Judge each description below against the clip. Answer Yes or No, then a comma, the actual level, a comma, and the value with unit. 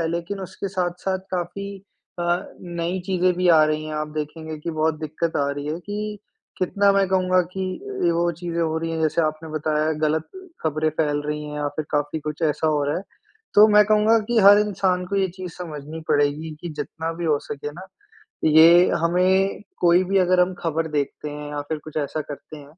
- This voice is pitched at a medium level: Yes, medium, 165 Hz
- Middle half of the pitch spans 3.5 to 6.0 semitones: No, average, 3.1 semitones